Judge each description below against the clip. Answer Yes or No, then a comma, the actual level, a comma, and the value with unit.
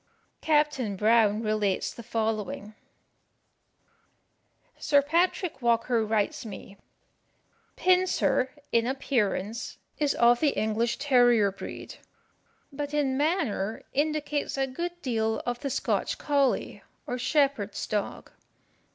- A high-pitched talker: Yes, high, 245 Hz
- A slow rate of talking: Yes, slow, 105 wpm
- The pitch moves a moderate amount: Yes, average, 4.9 semitones